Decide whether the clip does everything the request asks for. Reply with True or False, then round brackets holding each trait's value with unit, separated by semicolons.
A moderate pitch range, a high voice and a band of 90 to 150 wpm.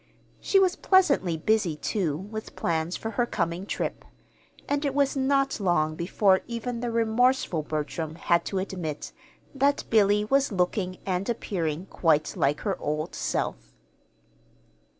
False (6.5 semitones; 195 Hz; 140 wpm)